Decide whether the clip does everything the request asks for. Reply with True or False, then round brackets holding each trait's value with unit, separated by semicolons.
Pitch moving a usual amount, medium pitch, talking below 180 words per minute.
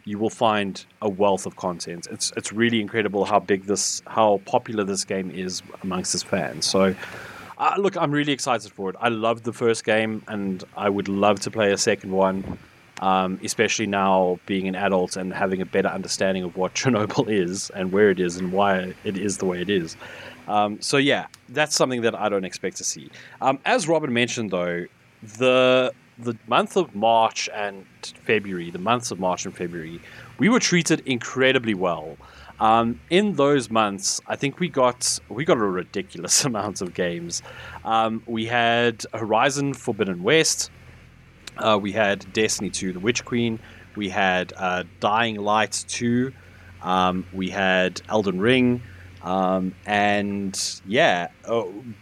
False (3.9 semitones; 105 Hz; 170 wpm)